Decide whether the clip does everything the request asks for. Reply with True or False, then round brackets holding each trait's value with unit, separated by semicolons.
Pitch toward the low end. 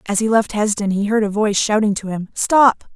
False (210 Hz)